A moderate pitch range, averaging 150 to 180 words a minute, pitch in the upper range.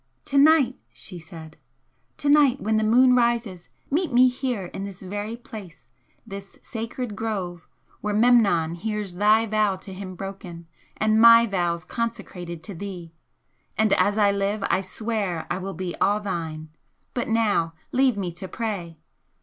Yes: average, 4.1 semitones; average, 160 wpm; high, 205 Hz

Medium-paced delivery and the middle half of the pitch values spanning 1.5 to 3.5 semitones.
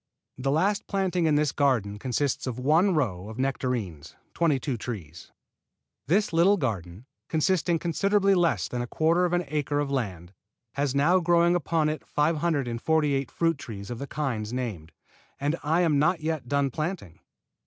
No: average, 165 wpm; wide, 5.5 semitones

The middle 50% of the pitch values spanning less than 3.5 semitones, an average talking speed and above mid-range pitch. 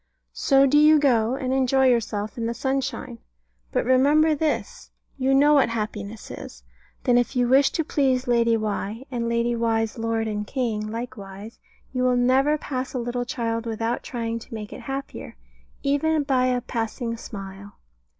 Yes: average, 2.9 semitones; average, 170 wpm; high, 245 Hz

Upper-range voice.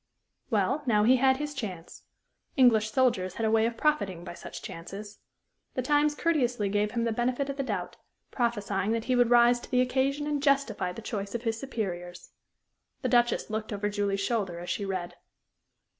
Yes: high, 230 Hz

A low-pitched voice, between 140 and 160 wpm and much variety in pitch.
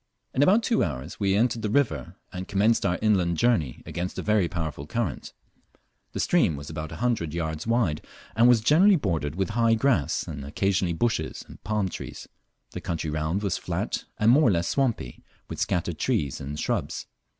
No: very low, 95 Hz; average, 185 wpm; wide, 6.6 semitones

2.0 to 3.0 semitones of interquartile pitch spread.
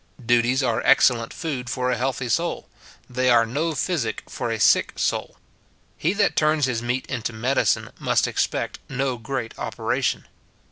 Yes: average, 2.7 semitones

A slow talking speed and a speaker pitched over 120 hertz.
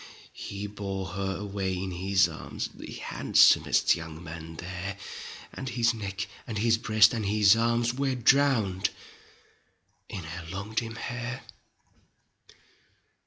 No: slow, 125 wpm; low, 100 Hz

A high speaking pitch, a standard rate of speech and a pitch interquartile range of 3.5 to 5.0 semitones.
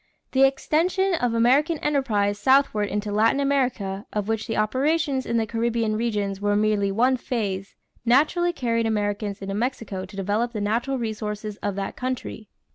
Yes: high, 225 Hz; average, 165 wpm; average, 4.2 semitones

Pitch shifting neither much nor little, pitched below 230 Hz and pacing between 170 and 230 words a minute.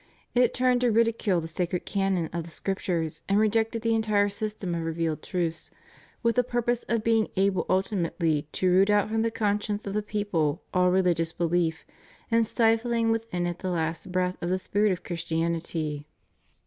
Yes: average, 4.6 semitones; high, 190 Hz; average, 175 wpm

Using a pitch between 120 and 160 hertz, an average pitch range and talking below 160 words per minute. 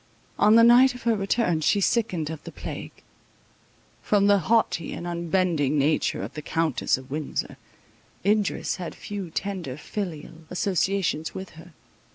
No: medium, 180 Hz; average, 4.4 semitones; average, 150 wpm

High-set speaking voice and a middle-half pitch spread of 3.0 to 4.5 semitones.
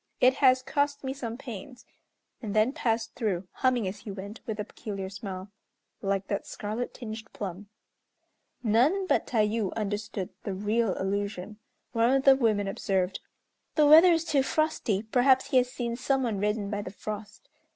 Yes: high, 220 Hz; average, 4.2 semitones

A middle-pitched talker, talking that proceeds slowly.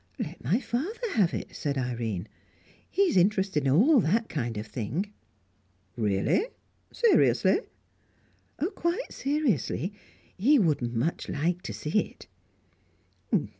Yes: medium, 180 Hz; slow, 120 wpm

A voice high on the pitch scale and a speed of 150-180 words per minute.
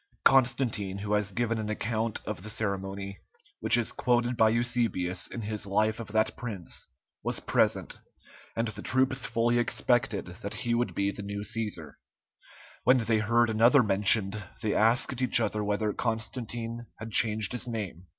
No: low, 110 Hz; average, 160 wpm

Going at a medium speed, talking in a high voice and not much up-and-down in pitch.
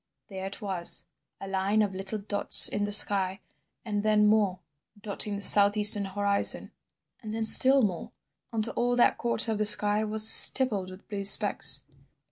Yes: average, 160 wpm; high, 205 Hz; narrow, 1.6 semitones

